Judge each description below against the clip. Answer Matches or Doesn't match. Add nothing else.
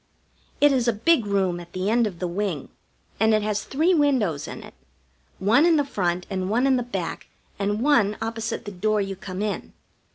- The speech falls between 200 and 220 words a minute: Matches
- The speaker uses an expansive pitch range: Doesn't match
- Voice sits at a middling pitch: Doesn't match